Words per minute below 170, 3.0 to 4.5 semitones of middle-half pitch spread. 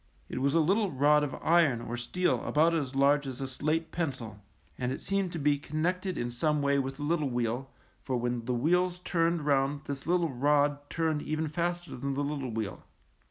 No: fast, 205 wpm; average, 3.8 semitones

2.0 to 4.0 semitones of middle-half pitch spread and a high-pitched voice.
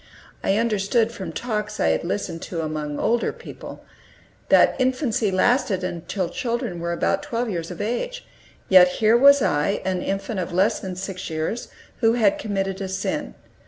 No: average, 4.5 semitones; high, 195 Hz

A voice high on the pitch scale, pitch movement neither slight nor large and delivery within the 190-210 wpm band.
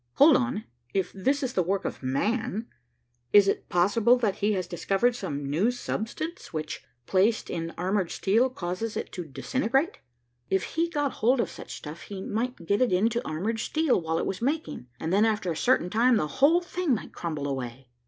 No: high, 210 Hz; wide, 6.2 semitones; average, 195 wpm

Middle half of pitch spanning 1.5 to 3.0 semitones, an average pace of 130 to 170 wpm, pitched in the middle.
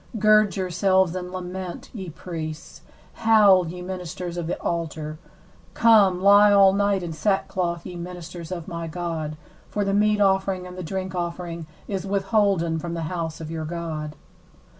Yes: narrow, 2.5 semitones; average, 160 wpm; medium, 180 Hz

